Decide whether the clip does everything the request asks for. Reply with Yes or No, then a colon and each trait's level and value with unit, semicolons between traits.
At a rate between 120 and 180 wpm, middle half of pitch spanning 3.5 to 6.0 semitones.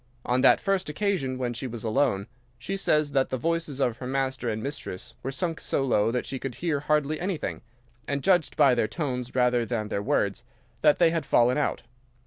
No: fast, 205 wpm; average, 4.0 semitones